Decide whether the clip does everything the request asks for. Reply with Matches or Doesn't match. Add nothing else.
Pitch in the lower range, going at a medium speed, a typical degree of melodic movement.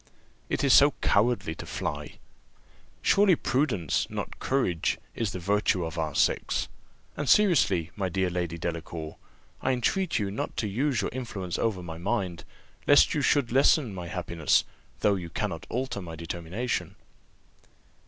Doesn't match